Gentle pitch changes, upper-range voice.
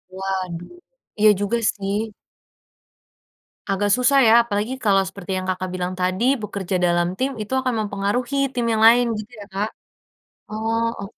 No: average, 3.3 semitones; high, 205 Hz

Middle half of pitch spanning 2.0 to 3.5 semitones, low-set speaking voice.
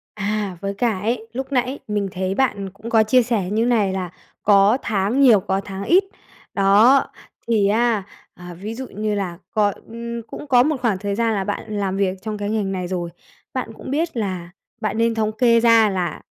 No: average, 3.1 semitones; high, 215 Hz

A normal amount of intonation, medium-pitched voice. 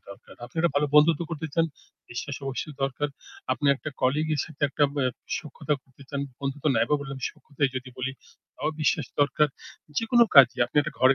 No: narrow, 2.3 semitones; medium, 145 Hz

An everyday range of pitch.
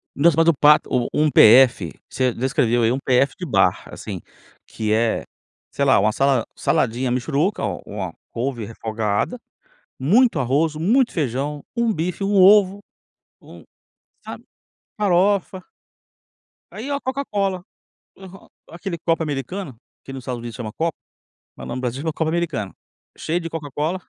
No: wide, 6.8 semitones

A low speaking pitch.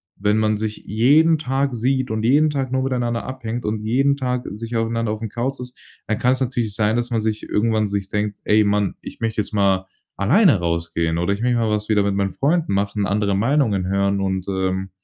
Yes: low, 110 Hz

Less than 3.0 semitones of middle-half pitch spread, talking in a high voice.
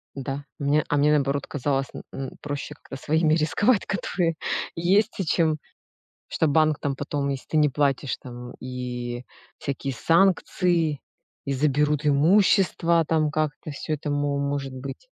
No: narrow, 2.4 semitones; medium, 145 Hz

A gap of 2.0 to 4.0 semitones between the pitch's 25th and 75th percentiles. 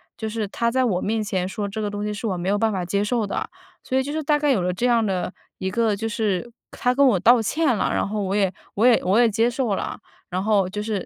Yes: average, 3.2 semitones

